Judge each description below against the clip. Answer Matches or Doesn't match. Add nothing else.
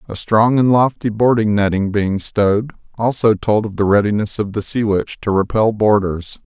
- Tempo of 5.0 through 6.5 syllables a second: Doesn't match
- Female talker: Doesn't match